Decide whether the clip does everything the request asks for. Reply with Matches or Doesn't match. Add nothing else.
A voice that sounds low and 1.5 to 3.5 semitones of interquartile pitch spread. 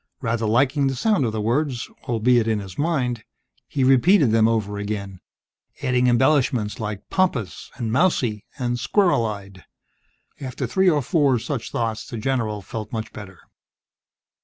Doesn't match